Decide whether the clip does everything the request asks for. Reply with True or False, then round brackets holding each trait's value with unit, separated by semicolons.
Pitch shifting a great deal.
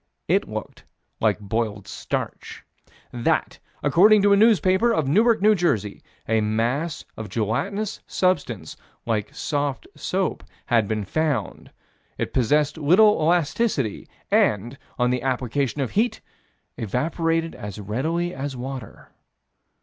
True (7.7 semitones)